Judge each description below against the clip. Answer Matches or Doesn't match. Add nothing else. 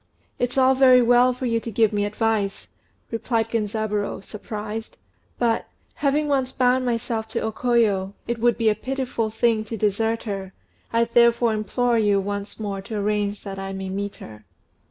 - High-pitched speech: Matches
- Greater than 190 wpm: Doesn't match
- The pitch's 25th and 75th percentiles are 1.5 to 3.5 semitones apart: Matches